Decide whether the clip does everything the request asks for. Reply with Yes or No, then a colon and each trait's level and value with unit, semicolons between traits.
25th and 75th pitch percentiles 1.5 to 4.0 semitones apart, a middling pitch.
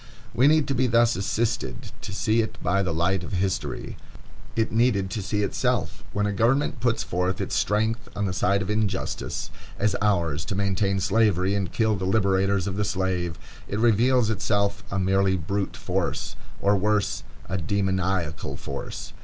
No: narrow, 2.6 semitones; low, 100 Hz